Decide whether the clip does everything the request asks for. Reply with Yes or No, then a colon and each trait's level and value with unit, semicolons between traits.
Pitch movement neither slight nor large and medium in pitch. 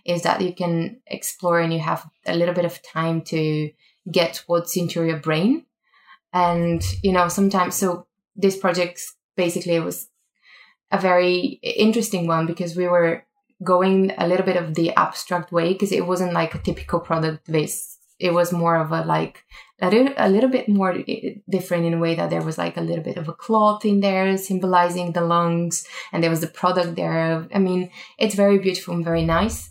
No: narrow, 2.2 semitones; medium, 175 Hz